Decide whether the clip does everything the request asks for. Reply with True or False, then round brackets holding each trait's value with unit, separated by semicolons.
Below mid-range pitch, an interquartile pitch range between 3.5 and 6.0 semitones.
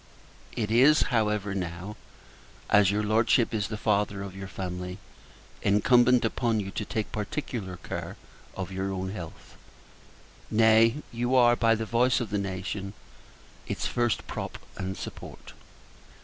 False (105 Hz; 3.1 semitones)